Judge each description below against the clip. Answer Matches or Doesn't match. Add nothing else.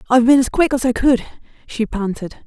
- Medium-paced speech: Doesn't match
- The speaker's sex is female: Matches